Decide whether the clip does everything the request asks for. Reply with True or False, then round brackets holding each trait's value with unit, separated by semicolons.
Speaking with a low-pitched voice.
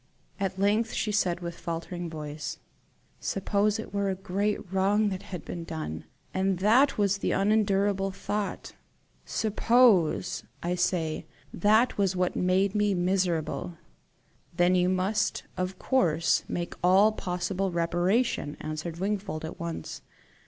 False (190 Hz)